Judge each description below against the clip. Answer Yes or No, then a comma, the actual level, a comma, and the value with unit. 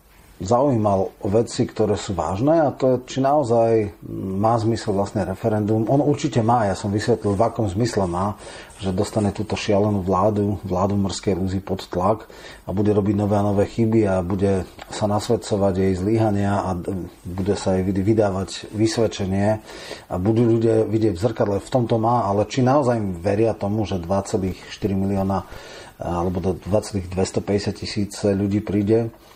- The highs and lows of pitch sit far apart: No, narrow, 2.5 semitones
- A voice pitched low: Yes, low, 105 Hz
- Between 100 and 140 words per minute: No, average, 160 wpm